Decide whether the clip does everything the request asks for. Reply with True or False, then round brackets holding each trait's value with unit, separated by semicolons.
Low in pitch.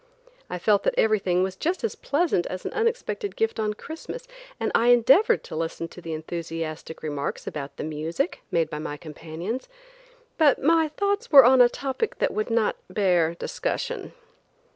False (210 Hz)